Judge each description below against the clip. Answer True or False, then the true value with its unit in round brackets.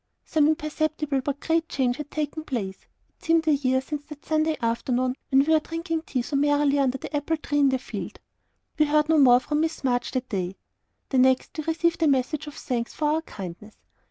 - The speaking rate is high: True (215 wpm)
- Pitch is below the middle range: False (290 Hz)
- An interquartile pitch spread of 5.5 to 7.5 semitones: False (3.3 semitones)